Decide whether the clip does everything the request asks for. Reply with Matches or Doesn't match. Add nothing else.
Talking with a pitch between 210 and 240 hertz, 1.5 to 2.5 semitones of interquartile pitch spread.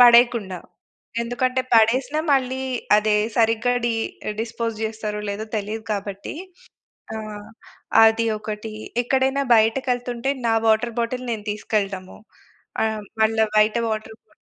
Matches